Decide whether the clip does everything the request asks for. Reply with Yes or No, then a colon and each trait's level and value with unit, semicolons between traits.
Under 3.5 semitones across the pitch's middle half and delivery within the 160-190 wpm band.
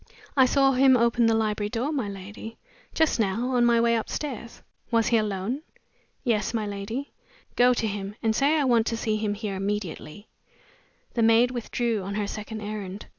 Yes: average, 2.8 semitones; average, 180 wpm